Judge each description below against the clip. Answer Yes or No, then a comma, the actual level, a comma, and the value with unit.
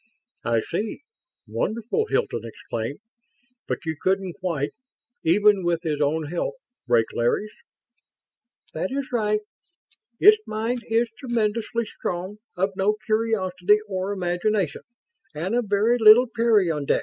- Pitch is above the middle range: Yes, high, 205 Hz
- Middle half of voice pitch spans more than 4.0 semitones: Yes, average, 4.5 semitones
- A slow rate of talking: Yes, slow, 120 wpm